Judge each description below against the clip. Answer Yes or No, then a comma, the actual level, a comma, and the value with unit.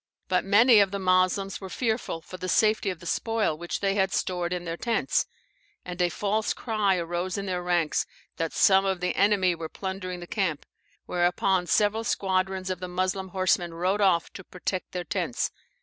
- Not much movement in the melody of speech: Yes, narrow, 1.9 semitones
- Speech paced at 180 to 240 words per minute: Yes, average, 190 wpm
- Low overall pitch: No, medium, 185 Hz